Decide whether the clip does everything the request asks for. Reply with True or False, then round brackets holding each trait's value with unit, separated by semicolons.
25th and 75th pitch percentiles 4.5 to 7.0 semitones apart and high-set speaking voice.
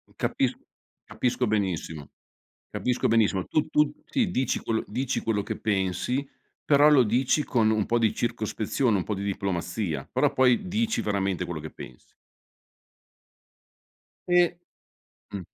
False (5.3 semitones; 110 Hz)